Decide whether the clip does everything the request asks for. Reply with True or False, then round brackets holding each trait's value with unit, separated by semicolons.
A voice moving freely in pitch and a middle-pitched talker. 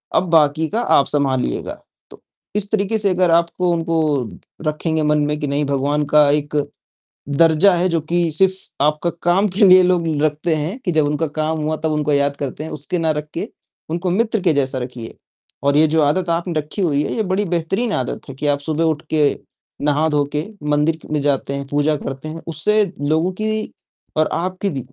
False (3.2 semitones; 155 Hz)